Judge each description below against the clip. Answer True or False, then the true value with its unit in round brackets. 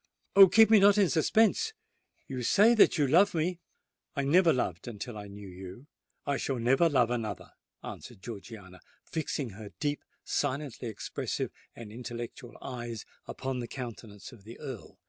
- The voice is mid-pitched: False (125 Hz)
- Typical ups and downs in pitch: False (6.2 semitones)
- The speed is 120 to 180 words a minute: True (155 wpm)